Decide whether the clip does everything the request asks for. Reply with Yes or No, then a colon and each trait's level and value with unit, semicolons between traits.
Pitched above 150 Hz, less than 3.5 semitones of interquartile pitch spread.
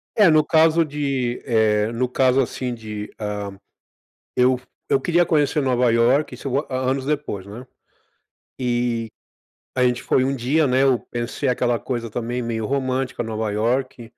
No: low, 125 Hz; average, 2.7 semitones